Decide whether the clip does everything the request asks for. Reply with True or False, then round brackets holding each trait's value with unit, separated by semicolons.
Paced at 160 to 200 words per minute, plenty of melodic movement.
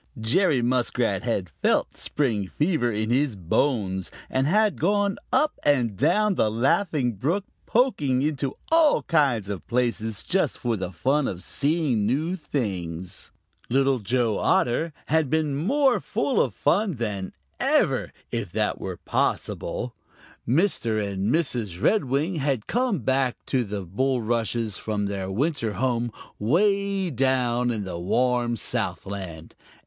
False (135 wpm; 6.3 semitones)